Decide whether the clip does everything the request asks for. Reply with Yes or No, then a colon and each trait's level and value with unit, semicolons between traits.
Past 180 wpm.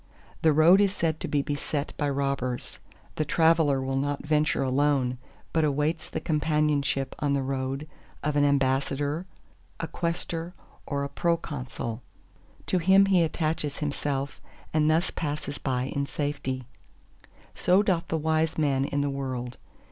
No: average, 150 wpm